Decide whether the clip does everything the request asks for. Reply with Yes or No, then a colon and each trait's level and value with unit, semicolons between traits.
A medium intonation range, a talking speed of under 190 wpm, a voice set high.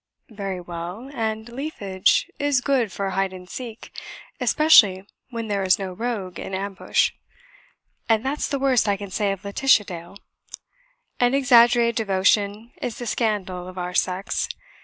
Yes: average, 4.2 semitones; average, 150 wpm; high, 205 Hz